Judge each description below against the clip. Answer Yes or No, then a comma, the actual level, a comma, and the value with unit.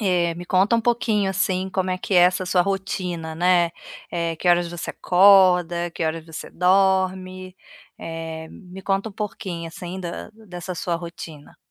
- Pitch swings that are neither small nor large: No, narrow, 1.9 semitones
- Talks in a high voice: No, medium, 180 Hz